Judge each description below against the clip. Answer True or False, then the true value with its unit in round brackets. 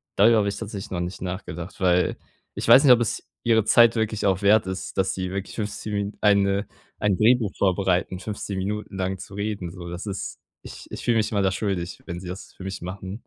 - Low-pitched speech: True (100 Hz)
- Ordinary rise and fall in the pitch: False (2.3 semitones)